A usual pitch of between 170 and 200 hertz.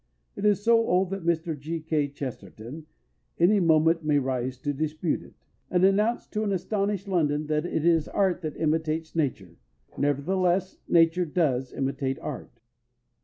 No: medium, 160 Hz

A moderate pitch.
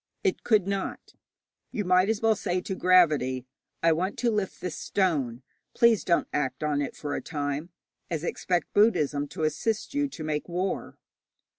Yes: medium, 175 Hz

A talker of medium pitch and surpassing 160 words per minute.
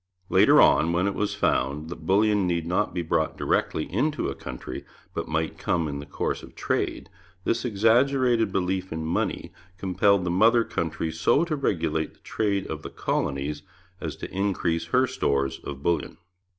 No: very low, 90 Hz; average, 175 wpm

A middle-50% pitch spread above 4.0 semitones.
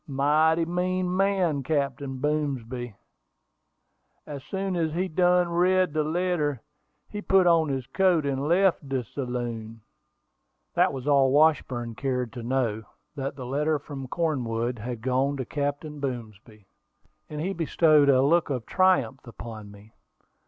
Yes: average, 4.8 semitones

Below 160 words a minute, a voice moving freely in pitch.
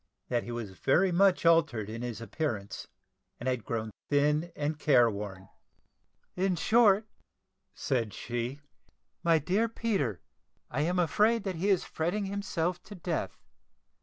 Yes: average, 140 wpm; wide, 7.8 semitones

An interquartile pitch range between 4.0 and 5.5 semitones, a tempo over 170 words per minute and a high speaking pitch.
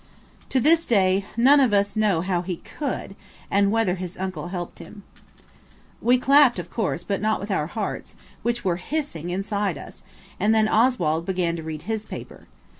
Yes: average, 4.3 semitones; average, 180 wpm; high, 200 Hz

